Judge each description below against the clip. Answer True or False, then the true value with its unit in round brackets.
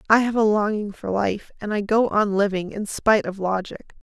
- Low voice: False (205 Hz)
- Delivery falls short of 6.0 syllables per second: True (5.2 syllables/s)